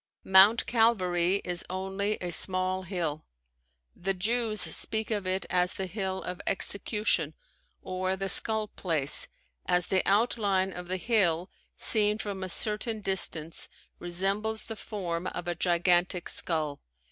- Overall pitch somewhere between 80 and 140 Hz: No, high, 190 Hz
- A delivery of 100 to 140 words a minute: Yes, slow, 135 wpm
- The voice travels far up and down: No, average, 2.9 semitones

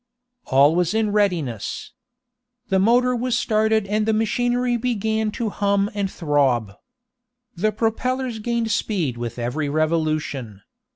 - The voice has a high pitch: Yes, high, 205 Hz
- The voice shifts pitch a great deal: Yes, wide, 6.4 semitones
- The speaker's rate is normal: No, slow, 125 wpm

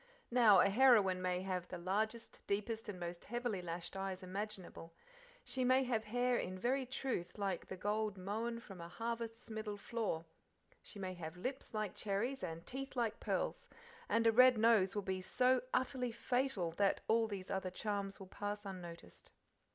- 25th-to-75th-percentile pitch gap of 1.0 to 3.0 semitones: No, average, 4.0 semitones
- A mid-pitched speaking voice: No, high, 210 Hz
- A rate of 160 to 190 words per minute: Yes, average, 175 wpm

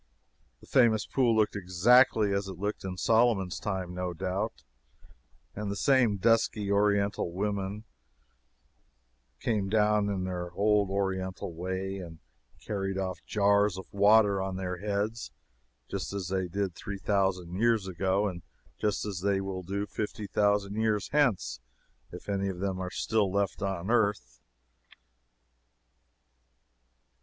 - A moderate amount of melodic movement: No, narrow, 2.0 semitones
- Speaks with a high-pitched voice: No, low, 100 Hz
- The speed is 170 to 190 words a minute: No, average, 140 wpm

